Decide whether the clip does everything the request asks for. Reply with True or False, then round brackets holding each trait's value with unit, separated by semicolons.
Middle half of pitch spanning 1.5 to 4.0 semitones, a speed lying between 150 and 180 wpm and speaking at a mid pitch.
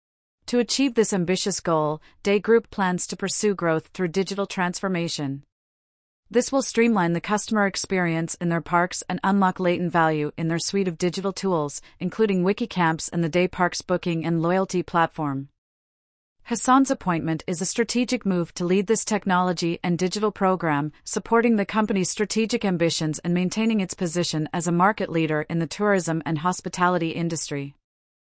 True (3.4 semitones; 160 wpm; 180 Hz)